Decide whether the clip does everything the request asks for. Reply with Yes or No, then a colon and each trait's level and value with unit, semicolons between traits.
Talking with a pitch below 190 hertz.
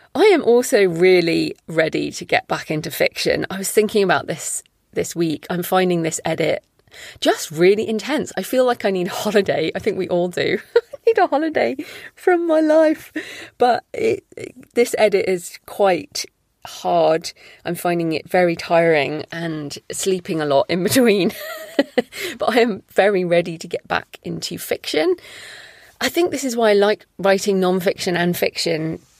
No: high, 205 Hz